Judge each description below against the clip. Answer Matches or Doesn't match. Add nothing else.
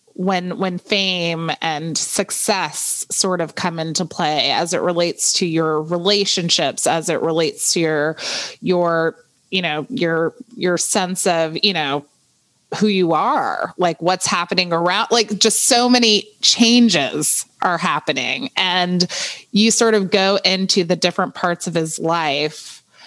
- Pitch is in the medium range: Matches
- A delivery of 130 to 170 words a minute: Matches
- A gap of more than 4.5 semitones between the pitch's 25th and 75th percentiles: Doesn't match